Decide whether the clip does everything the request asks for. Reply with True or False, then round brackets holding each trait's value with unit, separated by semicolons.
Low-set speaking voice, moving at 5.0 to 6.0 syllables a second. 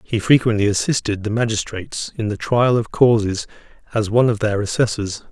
True (110 Hz; 5.5 syllables/s)